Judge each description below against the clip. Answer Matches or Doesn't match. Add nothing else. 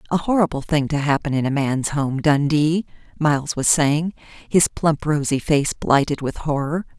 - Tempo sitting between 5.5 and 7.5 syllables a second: Doesn't match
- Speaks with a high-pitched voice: Doesn't match